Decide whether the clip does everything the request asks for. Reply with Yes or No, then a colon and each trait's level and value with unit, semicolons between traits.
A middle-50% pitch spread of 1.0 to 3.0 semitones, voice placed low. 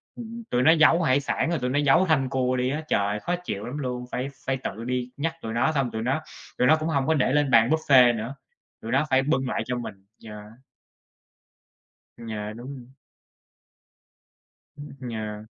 No: average, 3.9 semitones; low, 130 Hz